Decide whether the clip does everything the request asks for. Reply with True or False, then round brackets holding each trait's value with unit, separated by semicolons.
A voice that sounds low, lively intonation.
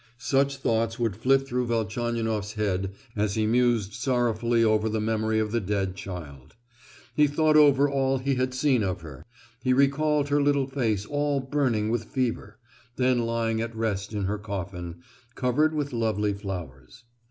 False (115 Hz; 4.3 semitones)